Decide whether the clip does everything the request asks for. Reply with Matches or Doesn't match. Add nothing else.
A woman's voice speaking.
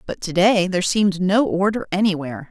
Matches